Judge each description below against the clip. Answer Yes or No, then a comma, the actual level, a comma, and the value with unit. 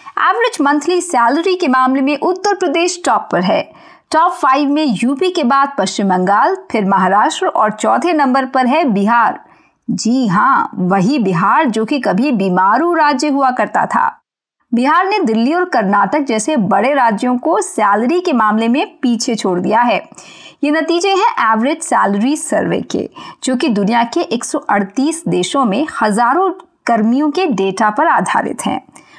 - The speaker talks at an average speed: Yes, average, 160 wpm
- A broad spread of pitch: Yes, wide, 6.5 semitones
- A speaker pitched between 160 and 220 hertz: No, very high, 270 Hz